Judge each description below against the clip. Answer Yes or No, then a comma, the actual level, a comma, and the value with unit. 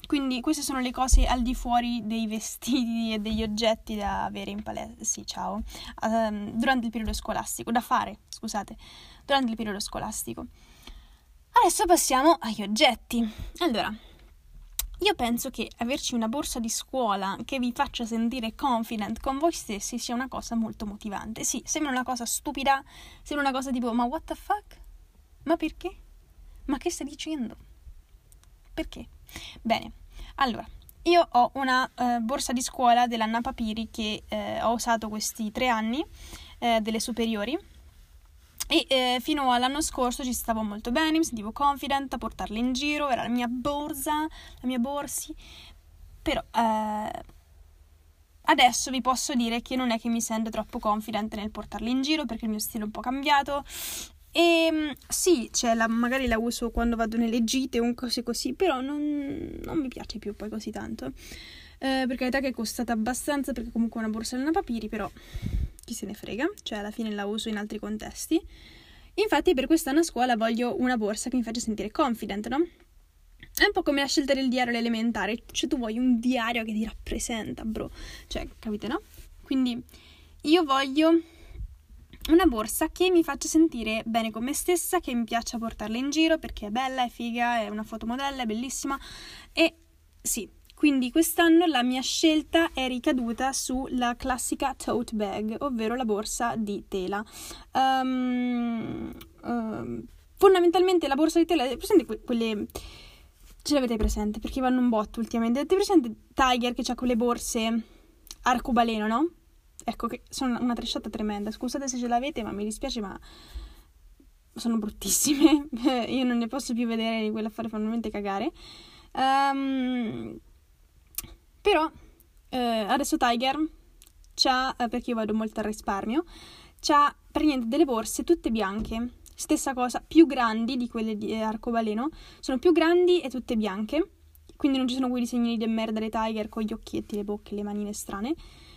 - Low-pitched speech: No, high, 245 Hz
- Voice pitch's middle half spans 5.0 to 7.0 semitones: No, average, 4.2 semitones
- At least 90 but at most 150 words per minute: No, average, 165 wpm